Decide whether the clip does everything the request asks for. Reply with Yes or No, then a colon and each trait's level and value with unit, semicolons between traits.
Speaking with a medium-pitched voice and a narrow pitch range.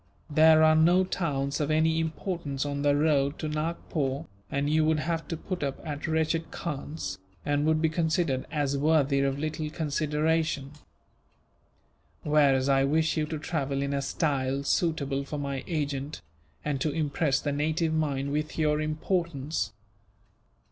Yes: medium, 150 Hz; narrow, 2.3 semitones